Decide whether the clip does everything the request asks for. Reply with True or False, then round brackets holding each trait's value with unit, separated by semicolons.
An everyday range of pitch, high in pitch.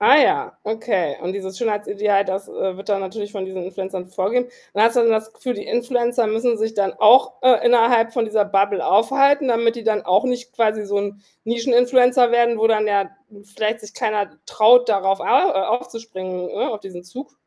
True (3.3 semitones; 220 Hz)